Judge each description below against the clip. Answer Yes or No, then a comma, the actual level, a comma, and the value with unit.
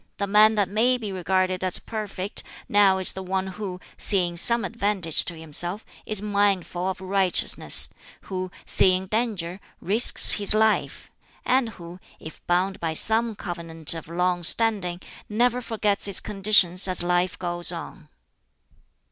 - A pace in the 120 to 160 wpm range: Yes, average, 145 wpm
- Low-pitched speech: No, high, 190 Hz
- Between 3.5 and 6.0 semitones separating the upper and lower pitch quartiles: No, average, 2.9 semitones